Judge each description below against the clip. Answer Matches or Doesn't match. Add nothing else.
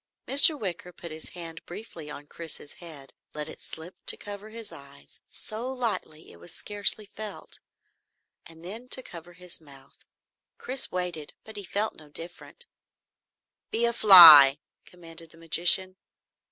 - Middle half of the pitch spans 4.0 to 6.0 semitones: Matches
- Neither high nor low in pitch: Matches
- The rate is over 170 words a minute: Doesn't match